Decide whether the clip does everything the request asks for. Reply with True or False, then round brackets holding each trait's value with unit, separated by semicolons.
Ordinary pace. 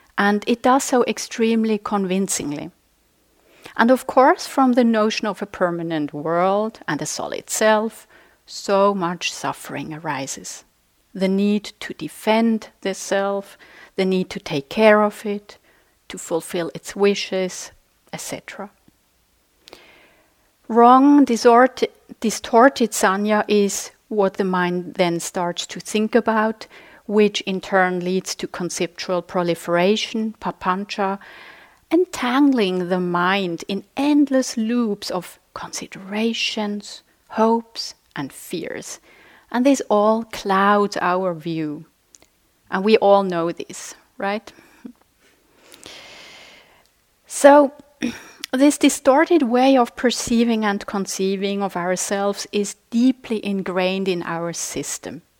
False (110 wpm)